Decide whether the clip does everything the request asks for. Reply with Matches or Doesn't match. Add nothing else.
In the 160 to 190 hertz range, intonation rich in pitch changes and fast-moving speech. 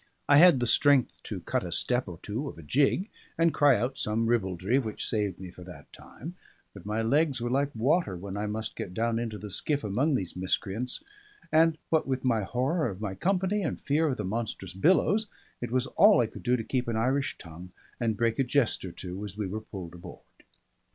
Doesn't match